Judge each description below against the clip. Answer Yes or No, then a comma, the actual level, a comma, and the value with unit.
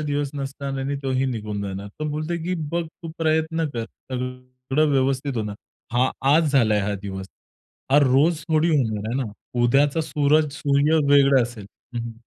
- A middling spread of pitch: Yes, average, 4.1 semitones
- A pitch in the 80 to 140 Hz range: Yes, low, 135 Hz